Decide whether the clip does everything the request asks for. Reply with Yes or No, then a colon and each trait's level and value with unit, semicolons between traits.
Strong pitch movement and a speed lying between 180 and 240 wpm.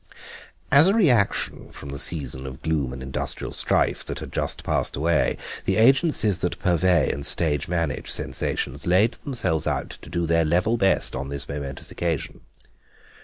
No: wide, 6.1 semitones; average, 165 wpm